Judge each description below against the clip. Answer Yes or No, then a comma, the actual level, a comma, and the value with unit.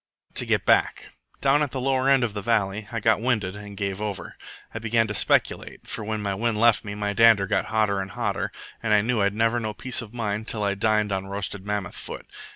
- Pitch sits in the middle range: No, low, 105 Hz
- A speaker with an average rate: No, fast, 240 wpm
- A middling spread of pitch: No, narrow, 2.2 semitones